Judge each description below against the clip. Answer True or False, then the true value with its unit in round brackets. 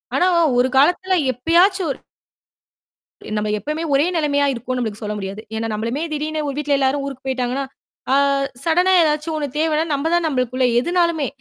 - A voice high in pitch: True (285 Hz)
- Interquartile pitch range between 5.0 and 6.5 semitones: False (4.2 semitones)